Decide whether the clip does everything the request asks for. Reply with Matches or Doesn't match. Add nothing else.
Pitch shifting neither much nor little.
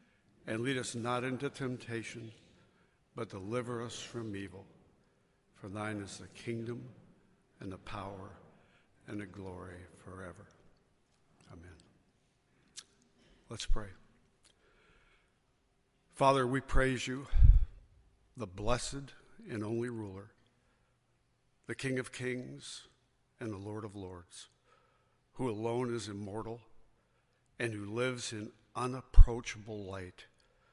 Matches